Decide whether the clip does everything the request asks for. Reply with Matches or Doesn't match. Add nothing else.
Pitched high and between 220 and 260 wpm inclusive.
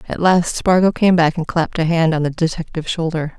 Doesn't match